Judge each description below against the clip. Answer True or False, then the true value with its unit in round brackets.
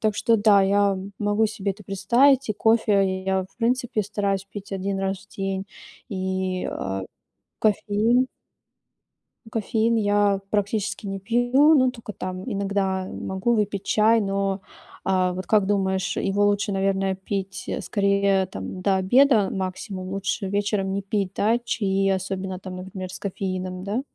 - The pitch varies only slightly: True (1.8 semitones)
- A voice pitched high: True (195 Hz)